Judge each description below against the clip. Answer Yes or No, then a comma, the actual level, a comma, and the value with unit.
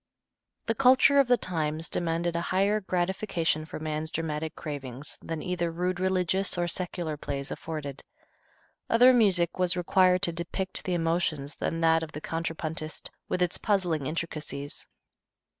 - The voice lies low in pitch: No, medium, 170 Hz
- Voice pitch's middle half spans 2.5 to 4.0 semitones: Yes, average, 2.8 semitones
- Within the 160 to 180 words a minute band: No, average, 145 wpm